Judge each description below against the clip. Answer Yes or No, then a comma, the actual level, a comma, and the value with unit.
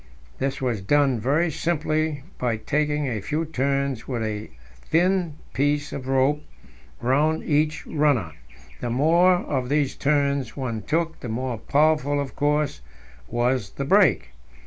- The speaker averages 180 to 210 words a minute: No, average, 140 wpm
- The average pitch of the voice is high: No, medium, 140 Hz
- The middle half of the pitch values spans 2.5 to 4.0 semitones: Yes, average, 3.4 semitones